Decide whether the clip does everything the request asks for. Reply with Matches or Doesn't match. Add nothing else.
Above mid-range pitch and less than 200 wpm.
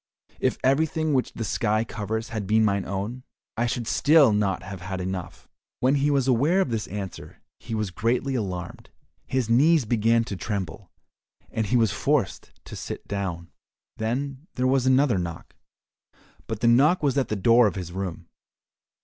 Doesn't match